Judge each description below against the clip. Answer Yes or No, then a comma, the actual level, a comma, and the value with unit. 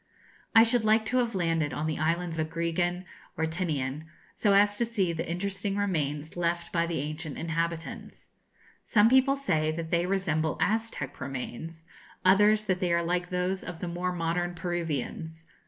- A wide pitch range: No, average, 3.4 semitones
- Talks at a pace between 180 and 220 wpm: No, average, 165 wpm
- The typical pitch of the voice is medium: Yes, medium, 175 Hz